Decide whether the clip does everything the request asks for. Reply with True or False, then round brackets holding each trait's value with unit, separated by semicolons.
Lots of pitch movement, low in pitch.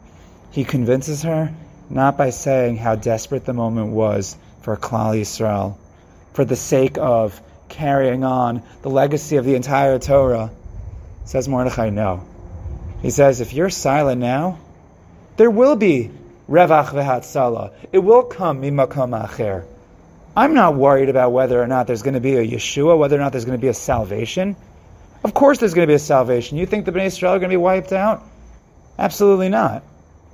True (5.7 semitones; 130 Hz)